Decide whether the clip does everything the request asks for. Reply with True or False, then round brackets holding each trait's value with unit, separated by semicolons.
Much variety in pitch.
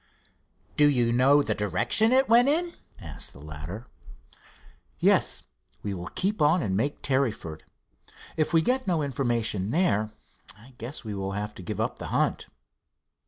True (7.8 semitones)